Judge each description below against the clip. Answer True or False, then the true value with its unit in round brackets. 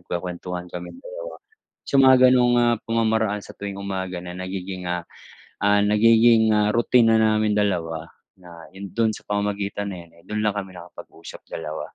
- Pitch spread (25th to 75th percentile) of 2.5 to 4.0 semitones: True (3.6 semitones)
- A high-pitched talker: False (100 Hz)